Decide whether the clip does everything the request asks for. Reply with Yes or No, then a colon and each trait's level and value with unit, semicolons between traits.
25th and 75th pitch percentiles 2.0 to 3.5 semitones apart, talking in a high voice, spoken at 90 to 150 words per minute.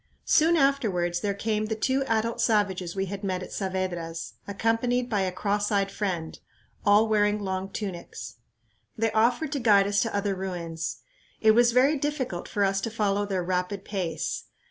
No: average, 3.2 semitones; high, 205 Hz; average, 170 wpm